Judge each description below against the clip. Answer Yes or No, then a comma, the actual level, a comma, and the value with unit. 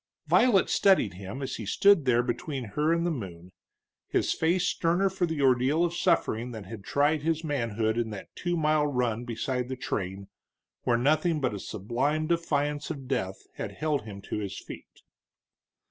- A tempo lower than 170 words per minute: No, average, 175 wpm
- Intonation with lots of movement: Yes, wide, 6.2 semitones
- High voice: No, low, 135 Hz